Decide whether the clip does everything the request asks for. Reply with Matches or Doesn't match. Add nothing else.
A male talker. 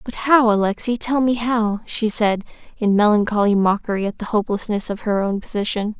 Doesn't match